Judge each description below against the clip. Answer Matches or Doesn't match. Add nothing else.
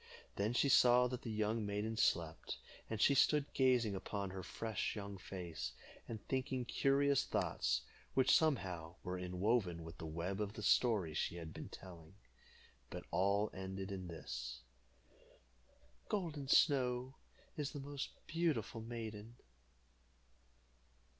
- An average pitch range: Doesn't match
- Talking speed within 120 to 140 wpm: Matches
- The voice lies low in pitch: Matches